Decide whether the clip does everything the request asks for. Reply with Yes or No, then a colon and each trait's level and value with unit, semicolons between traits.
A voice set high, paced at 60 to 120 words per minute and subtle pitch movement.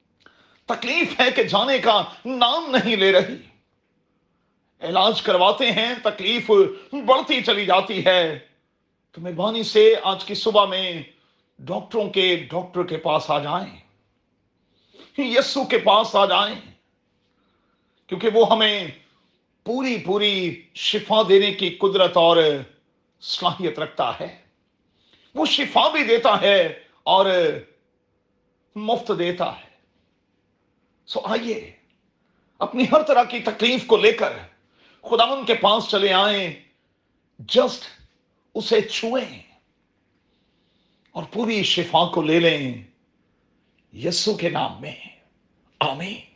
No: high, 210 Hz; average, 115 wpm; average, 4.9 semitones